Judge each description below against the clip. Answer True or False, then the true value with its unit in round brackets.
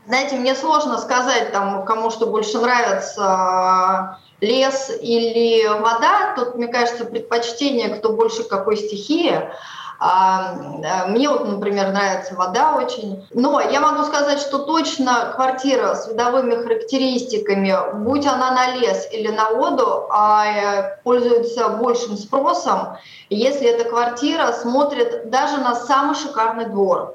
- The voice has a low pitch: False (235 Hz)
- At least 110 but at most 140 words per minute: True (120 wpm)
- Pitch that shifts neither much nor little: True (3.9 semitones)